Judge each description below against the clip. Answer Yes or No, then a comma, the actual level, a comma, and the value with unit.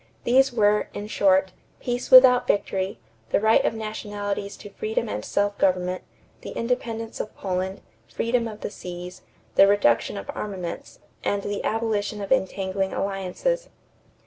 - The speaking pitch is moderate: No, high, 205 Hz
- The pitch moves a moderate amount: Yes, average, 3.0 semitones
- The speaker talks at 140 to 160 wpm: Yes, average, 145 wpm